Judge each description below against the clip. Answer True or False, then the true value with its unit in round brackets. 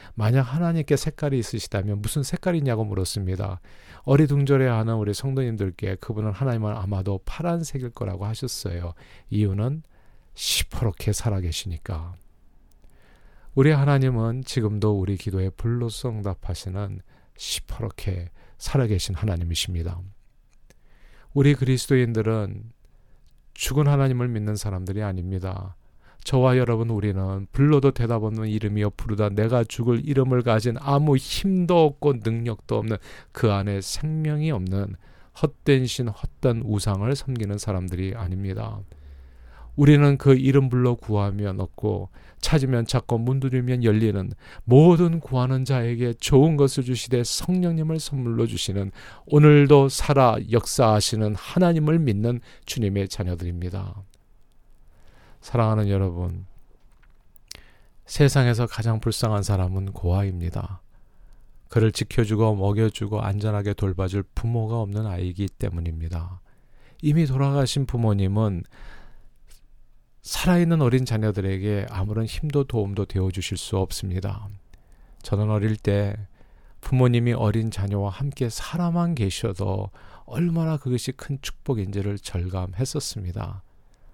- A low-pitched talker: True (110 Hz)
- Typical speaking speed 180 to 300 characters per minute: True (295 characters per minute)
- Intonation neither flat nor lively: True (4.9 semitones)